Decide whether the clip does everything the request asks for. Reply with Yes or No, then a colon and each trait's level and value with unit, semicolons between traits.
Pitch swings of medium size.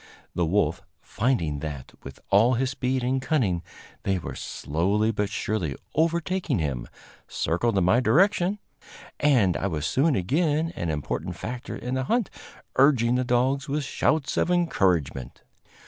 No: wide, 8.0 semitones